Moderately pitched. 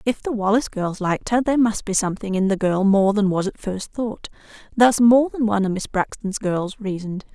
No: high, 210 Hz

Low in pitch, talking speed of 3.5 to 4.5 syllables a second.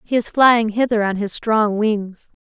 No: high, 220 Hz; 4.0 syllables/s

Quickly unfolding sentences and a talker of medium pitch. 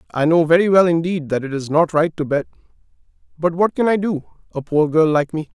Yes: fast, 235 wpm; medium, 165 Hz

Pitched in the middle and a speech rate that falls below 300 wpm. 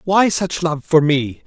Yes: medium, 165 Hz; fast, 205 wpm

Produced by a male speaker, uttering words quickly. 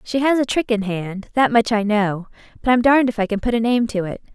No: female; fast, 275 wpm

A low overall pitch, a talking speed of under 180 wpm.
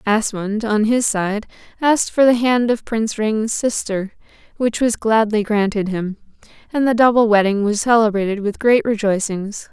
No: high, 220 Hz; average, 160 wpm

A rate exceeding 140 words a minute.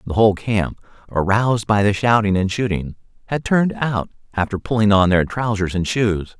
Yes: average, 180 wpm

